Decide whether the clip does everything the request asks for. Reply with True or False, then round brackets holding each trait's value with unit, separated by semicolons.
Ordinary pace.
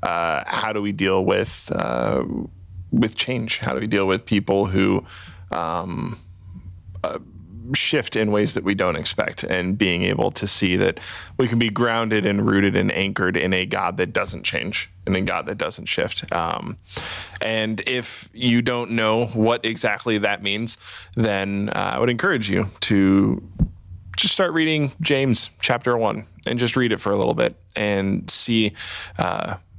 True (170 wpm)